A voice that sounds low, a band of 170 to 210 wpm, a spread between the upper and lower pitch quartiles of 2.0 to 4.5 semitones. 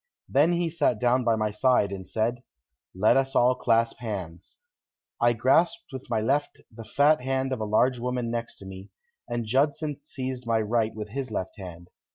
Yes: low, 120 Hz; average, 190 wpm; average, 3.5 semitones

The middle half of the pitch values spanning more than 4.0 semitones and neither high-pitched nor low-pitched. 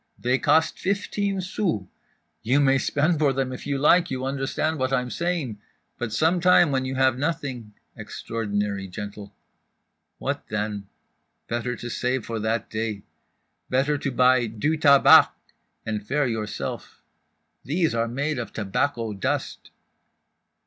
No: average, 4.7 semitones; low, 130 Hz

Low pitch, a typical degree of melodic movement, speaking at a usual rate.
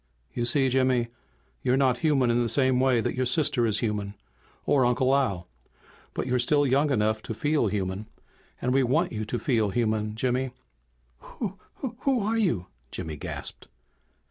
Yes: low, 125 Hz; average, 3.7 semitones; average, 170 wpm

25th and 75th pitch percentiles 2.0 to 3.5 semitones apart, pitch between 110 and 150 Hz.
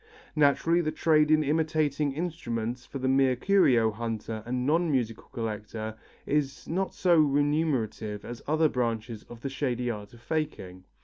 No: average, 5.1 semitones; low, 135 Hz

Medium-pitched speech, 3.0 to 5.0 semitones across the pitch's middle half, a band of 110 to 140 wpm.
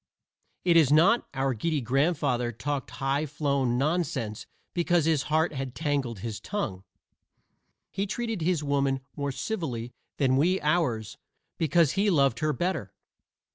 Yes: medium, 145 Hz; average, 4.4 semitones; slow, 135 wpm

